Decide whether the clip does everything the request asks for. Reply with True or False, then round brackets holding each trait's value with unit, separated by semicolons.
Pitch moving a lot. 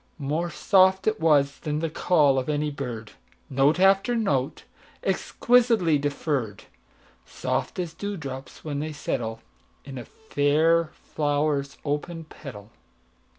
False (3.5 semitones)